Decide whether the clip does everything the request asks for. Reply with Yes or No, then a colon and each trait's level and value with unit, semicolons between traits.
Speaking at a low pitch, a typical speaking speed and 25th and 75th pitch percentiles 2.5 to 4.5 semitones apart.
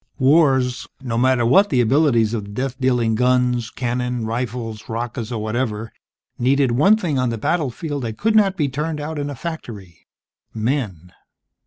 Yes: low, 125 Hz; average, 165 wpm; average, 3.8 semitones